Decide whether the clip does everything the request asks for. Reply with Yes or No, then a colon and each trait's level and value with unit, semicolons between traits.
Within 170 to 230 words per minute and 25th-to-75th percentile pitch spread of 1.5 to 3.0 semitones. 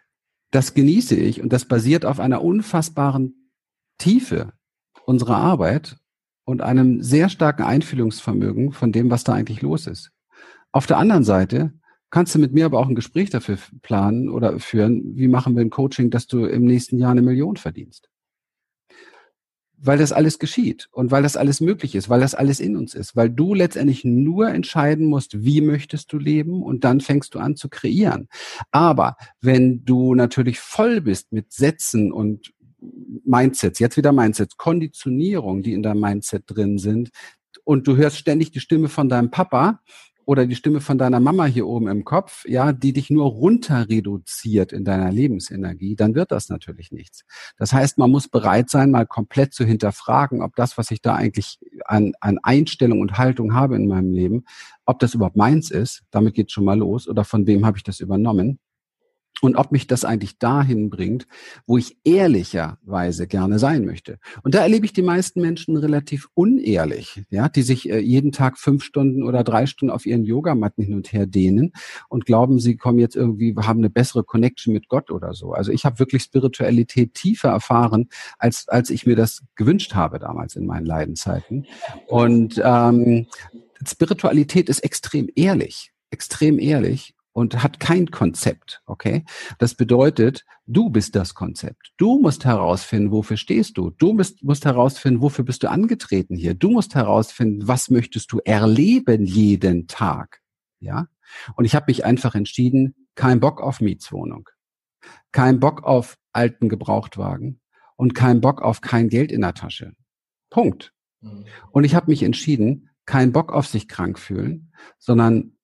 No: average, 175 wpm; average, 4.3 semitones